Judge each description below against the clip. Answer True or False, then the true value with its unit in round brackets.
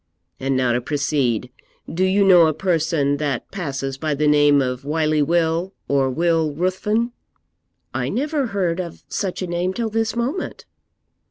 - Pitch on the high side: False (160 Hz)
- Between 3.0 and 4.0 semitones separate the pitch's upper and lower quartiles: False (4.8 semitones)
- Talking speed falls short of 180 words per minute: True (160 wpm)